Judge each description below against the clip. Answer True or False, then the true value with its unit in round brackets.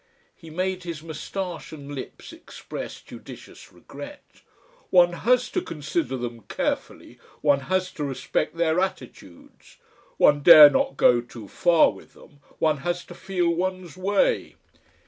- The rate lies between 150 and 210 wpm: False (140 wpm)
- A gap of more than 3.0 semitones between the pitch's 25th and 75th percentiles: True (4.2 semitones)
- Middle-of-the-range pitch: True (165 Hz)